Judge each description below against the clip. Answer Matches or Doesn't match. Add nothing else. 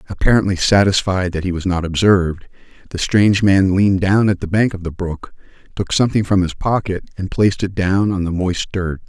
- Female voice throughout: Doesn't match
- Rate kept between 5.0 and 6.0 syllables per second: Matches